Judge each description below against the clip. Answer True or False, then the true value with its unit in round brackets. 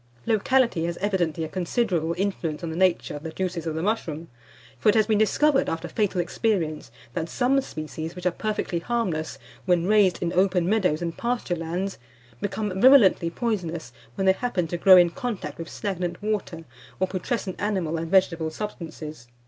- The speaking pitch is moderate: True (180 Hz)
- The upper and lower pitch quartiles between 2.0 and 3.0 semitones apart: False (4.0 semitones)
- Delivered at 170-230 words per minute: True (175 wpm)